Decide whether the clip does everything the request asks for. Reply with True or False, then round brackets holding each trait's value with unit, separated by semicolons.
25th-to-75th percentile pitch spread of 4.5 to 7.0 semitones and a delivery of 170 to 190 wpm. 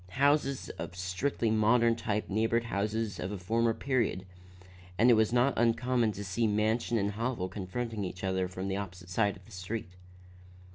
False (3.6 semitones; 175 wpm)